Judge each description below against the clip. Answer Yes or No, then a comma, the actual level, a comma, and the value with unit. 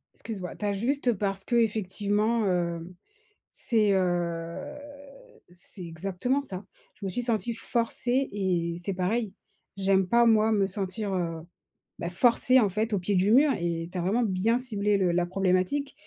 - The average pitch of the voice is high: Yes, high, 200 Hz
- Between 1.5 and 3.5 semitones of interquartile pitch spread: No, average, 4.0 semitones